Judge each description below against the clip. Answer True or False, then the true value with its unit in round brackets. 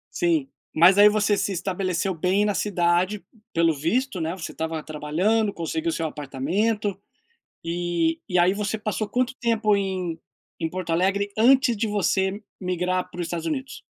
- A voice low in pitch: False (185 Hz)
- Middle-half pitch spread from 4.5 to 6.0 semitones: False (3.8 semitones)